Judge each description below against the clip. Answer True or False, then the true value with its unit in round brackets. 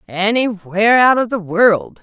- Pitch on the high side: True (205 Hz)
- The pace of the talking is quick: False (150 wpm)